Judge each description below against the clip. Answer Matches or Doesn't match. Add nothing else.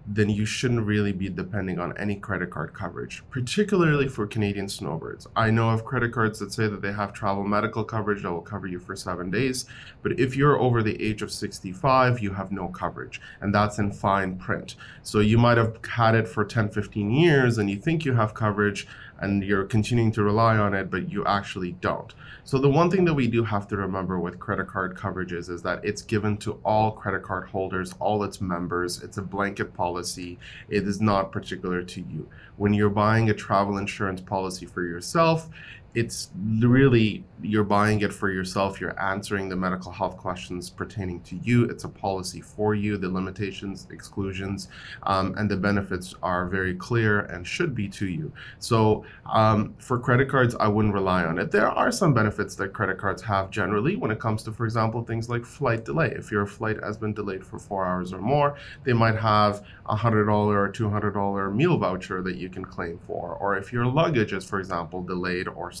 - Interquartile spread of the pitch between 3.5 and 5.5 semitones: Doesn't match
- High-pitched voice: Doesn't match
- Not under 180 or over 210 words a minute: Matches